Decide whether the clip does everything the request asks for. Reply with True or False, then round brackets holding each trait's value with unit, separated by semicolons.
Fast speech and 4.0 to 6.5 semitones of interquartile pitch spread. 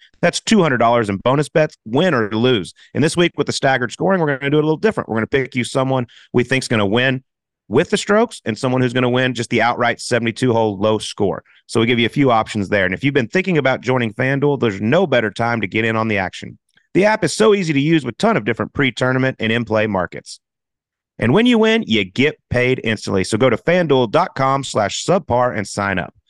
True (245 wpm; 4.3 semitones)